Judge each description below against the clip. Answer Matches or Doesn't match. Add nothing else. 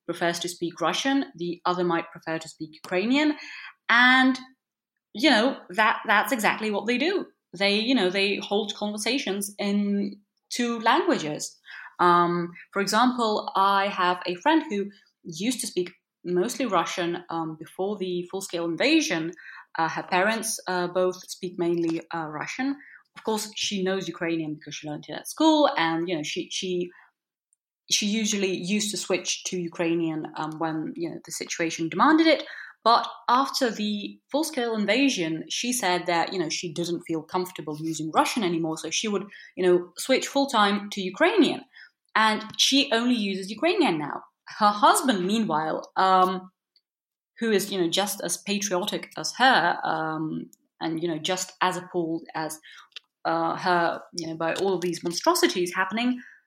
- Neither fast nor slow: Matches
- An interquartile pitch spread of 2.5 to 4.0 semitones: Doesn't match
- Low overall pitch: Doesn't match